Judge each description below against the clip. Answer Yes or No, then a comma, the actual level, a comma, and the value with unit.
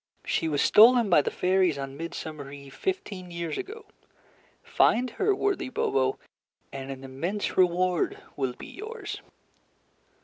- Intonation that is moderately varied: No, wide, 9.0 semitones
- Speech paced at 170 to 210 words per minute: No, slow, 135 wpm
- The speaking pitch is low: No, medium, 175 Hz